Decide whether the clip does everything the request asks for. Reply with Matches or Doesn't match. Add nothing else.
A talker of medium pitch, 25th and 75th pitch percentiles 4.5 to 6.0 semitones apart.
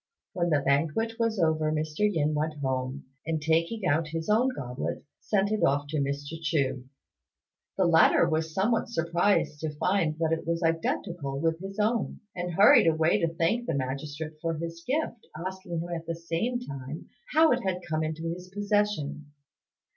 Doesn't match